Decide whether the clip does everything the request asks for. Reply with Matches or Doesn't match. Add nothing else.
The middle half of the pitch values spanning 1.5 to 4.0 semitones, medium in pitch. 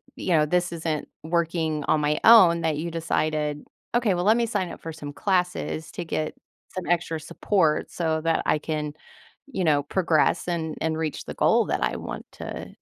Matches